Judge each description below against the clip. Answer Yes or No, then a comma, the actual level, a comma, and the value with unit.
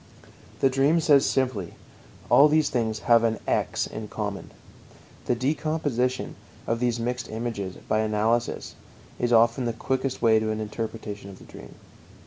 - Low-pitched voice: Yes, low, 115 Hz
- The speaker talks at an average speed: Yes, average, 150 wpm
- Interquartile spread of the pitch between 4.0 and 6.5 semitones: No, average, 3.0 semitones